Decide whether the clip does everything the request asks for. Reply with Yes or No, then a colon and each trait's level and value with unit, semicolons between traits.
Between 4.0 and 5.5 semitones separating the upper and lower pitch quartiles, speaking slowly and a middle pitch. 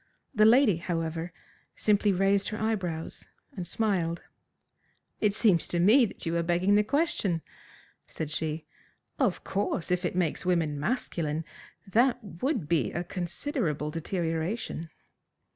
Yes: average, 4.3 semitones; slow, 130 wpm; medium, 180 Hz